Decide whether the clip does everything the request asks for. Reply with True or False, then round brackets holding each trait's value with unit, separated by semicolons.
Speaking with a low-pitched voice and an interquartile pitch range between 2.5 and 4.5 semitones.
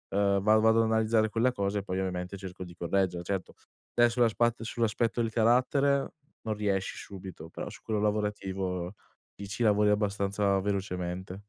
True (100 Hz; 2.8 semitones)